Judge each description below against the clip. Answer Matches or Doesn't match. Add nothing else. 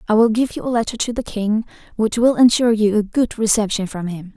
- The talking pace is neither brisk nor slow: Doesn't match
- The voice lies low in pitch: Doesn't match